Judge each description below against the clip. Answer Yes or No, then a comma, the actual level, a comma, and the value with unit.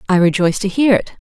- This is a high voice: Yes, high, 195 Hz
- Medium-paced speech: No, fast, 235 wpm